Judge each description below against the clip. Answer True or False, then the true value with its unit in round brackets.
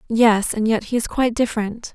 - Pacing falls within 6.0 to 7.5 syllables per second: False (5.7 syllables/s)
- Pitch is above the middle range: True (225 Hz)